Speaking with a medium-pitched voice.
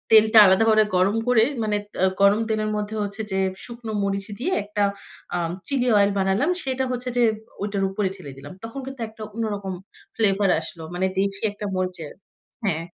No: high, 205 Hz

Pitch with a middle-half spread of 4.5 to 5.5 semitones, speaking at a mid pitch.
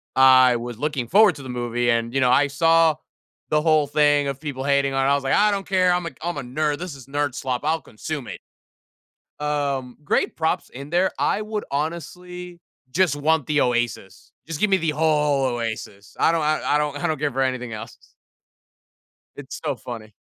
No: average, 3.8 semitones; medium, 145 Hz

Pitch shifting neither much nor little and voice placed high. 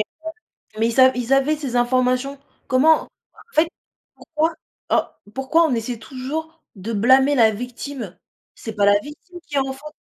Yes: average, 3.7 semitones; very high, 265 Hz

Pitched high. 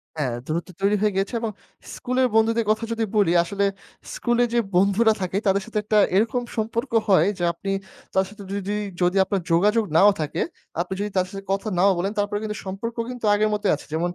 Yes: high, 205 Hz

